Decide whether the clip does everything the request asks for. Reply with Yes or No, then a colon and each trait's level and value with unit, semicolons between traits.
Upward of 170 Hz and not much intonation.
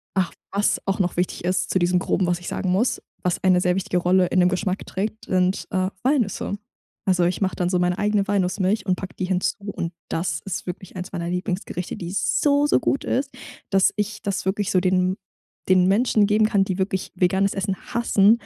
Yes: high, 190 Hz; narrow, 1.8 semitones